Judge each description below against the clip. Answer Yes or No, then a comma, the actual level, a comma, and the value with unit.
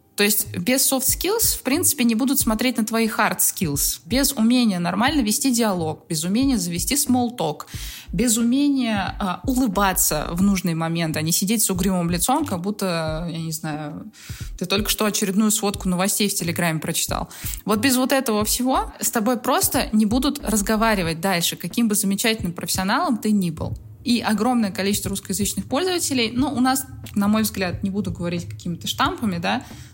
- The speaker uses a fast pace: Yes, fast, 175 wpm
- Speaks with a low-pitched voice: No, high, 210 Hz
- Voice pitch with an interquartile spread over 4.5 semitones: Yes, average, 5.1 semitones